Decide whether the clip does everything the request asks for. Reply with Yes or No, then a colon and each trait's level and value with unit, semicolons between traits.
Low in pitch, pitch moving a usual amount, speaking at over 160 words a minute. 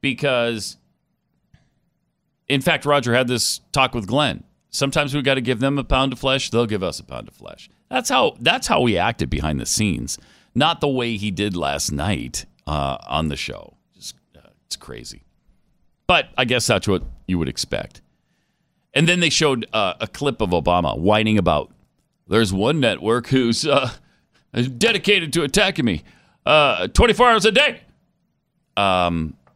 No: low, 120 Hz; wide, 7.3 semitones; average, 170 wpm